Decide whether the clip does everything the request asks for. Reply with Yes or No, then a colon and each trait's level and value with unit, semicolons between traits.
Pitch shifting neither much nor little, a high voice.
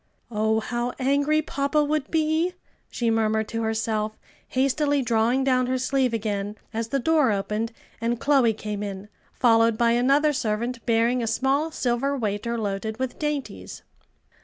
Yes: average, 3.9 semitones; high, 240 Hz